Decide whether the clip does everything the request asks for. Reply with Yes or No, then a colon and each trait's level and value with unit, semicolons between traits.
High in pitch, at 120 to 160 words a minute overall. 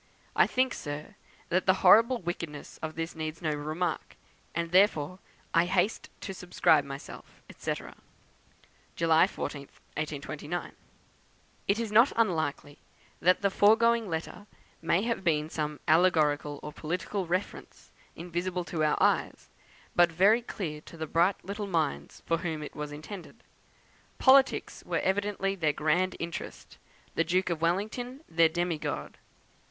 No: medium, 170 Hz; average, 140 wpm